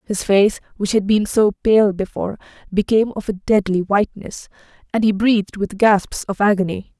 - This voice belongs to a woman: Yes, female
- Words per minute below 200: Yes, average, 170 wpm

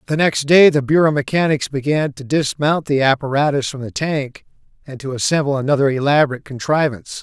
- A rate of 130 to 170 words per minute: Yes, average, 165 wpm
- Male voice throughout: Yes, male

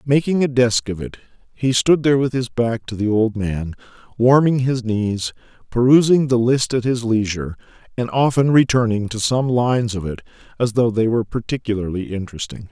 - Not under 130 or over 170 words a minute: No, average, 180 wpm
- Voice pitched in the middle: No, low, 120 Hz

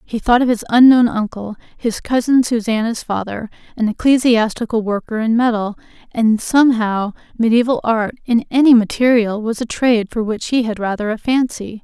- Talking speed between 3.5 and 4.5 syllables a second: No, 5.2 syllables/s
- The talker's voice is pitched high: Yes, high, 230 Hz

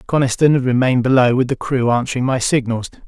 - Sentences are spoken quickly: No, average, 195 wpm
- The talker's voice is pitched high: No, low, 125 Hz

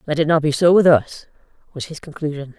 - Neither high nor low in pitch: Yes, medium, 150 Hz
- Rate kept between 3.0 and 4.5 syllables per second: No, 6.1 syllables/s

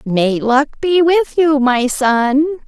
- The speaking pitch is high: Yes, very high, 280 Hz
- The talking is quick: No, average, 155 wpm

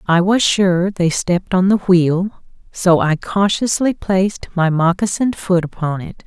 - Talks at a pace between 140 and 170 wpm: Yes, average, 165 wpm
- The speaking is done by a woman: Yes, female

